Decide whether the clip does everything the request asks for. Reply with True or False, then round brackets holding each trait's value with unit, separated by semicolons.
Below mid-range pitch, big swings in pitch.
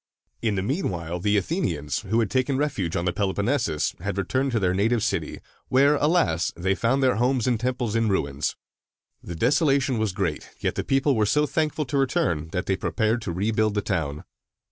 True (110 Hz; 6.4 semitones)